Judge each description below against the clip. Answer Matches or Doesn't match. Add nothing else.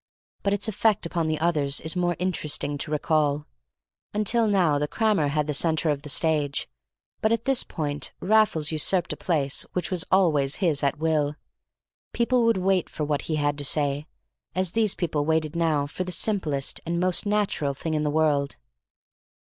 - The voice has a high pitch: Doesn't match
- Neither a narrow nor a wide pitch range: Matches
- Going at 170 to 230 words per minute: Matches